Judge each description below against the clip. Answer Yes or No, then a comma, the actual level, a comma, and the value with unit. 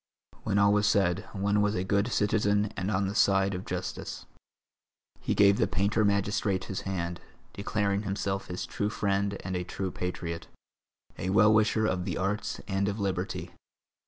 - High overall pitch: No, low, 100 Hz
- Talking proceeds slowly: No, average, 170 wpm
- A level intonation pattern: Yes, narrow, 1.5 semitones